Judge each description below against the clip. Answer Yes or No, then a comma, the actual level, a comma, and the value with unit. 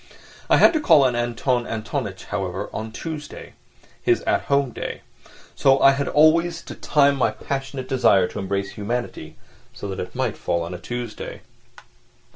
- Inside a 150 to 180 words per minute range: Yes, average, 160 wpm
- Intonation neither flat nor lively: Yes, average, 4.9 semitones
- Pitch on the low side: Yes, low, 125 Hz